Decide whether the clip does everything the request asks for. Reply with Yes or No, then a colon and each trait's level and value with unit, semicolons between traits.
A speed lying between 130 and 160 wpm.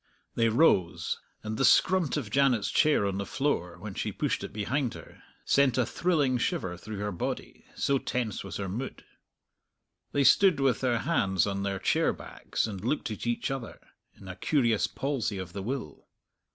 No: average, 180 wpm